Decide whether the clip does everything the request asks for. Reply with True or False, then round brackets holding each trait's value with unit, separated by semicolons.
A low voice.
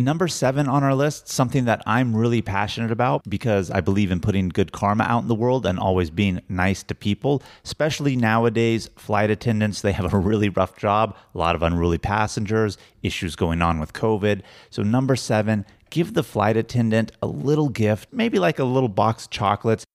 True (110 Hz)